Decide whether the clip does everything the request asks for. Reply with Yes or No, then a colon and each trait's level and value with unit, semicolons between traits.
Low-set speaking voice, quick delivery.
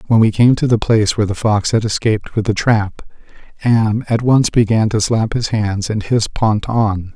Yes: low, 110 Hz; fast, 220 wpm